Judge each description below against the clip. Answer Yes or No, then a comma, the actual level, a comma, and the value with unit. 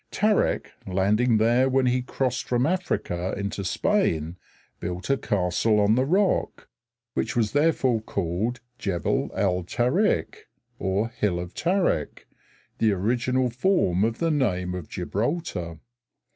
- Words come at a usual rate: No, slow, 120 wpm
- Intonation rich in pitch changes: Yes, wide, 5.8 semitones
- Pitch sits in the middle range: No, low, 115 Hz